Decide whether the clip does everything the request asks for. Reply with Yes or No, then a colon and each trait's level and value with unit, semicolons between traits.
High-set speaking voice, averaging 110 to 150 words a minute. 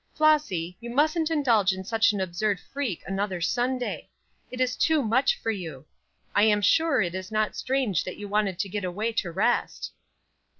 No: high, 215 Hz; average, 180 wpm